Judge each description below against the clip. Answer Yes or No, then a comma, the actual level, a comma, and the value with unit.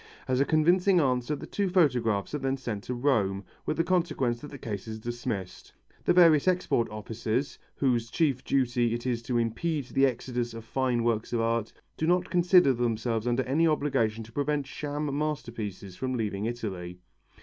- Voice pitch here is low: Yes, low, 125 Hz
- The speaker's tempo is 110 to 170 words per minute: No, average, 180 wpm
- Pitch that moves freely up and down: No, average, 4.5 semitones